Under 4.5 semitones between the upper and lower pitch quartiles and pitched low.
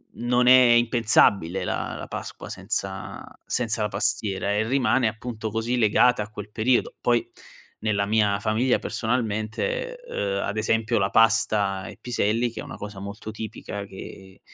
Yes: average, 2.7 semitones; low, 110 Hz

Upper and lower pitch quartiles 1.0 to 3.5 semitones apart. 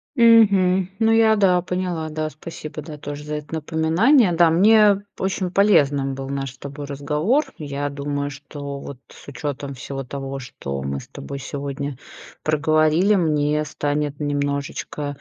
No: average, 4.1 semitones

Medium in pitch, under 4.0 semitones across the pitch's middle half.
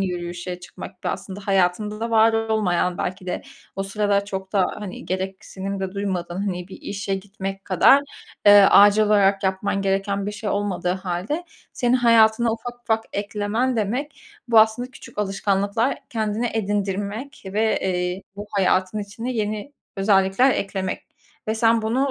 No: high, 200 Hz; narrow, 2.4 semitones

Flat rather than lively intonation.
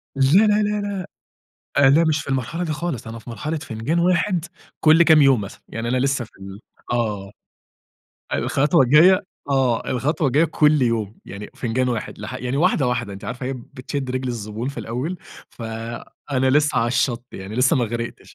No: average, 4.6 semitones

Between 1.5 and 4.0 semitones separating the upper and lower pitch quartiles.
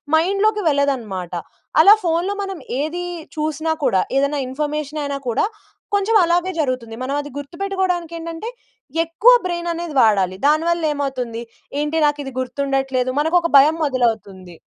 No: average, 4.7 semitones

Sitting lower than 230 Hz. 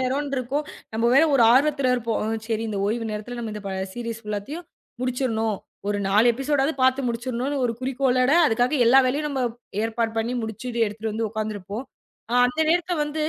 No: high, 245 Hz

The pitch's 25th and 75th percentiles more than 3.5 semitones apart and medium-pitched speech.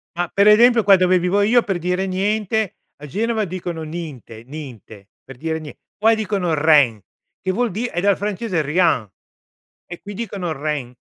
Yes: average, 5.0 semitones; medium, 180 Hz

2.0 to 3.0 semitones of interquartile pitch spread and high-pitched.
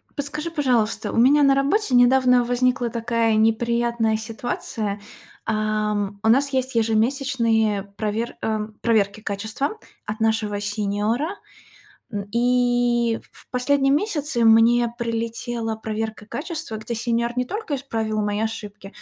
Yes: narrow, 2.5 semitones; high, 230 Hz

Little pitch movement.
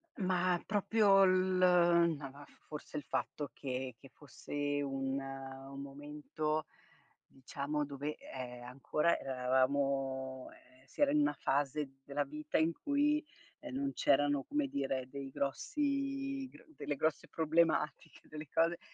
No: average, 4.9 semitones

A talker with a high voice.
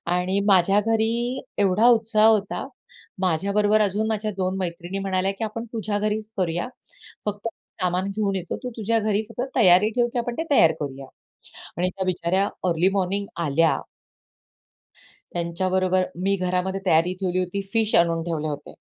Yes: high, 195 Hz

